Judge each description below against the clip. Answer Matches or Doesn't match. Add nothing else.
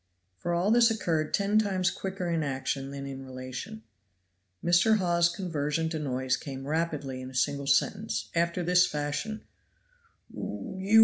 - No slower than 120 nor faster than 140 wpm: Doesn't match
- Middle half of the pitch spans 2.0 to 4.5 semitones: Doesn't match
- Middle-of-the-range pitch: Matches